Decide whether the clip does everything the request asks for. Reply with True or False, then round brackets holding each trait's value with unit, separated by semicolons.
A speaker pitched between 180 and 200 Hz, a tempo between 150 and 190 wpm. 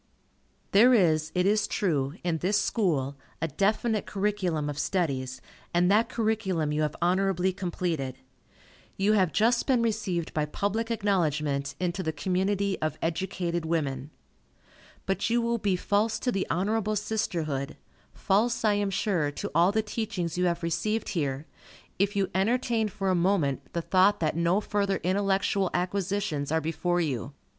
True (185 Hz; 155 wpm)